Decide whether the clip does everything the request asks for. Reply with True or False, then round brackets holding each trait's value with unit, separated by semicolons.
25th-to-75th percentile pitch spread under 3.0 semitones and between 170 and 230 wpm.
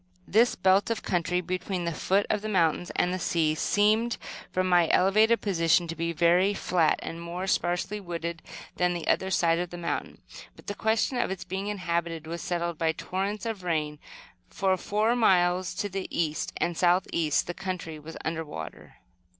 True (2.6 semitones; 190 wpm)